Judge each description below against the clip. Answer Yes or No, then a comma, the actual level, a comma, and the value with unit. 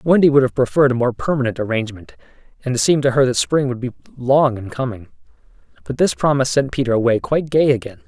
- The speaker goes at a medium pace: No, fast, 215 wpm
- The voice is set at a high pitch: No, low, 125 Hz